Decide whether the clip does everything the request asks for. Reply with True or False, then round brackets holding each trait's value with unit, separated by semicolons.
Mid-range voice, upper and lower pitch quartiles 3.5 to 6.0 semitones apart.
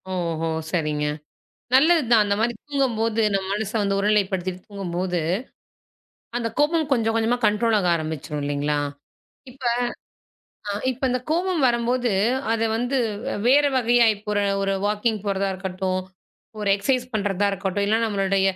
False (210 Hz; 4.1 semitones)